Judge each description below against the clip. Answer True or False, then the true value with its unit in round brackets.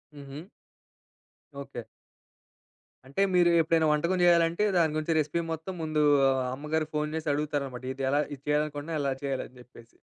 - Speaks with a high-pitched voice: False (150 Hz)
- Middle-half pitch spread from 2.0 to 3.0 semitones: True (2.6 semitones)